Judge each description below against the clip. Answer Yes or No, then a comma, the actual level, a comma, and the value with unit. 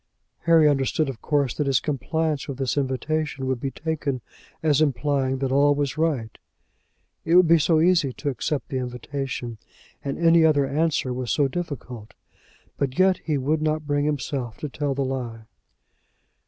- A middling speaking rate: Yes, average, 170 wpm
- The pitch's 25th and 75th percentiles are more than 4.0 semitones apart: No, average, 2.9 semitones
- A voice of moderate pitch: Yes, medium, 145 Hz